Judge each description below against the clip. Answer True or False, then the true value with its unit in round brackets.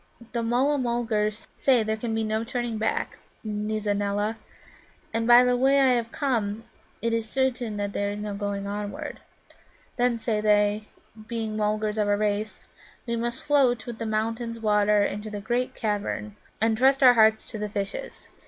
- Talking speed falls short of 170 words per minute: False (175 wpm)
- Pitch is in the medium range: False (220 Hz)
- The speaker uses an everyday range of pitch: False (2.3 semitones)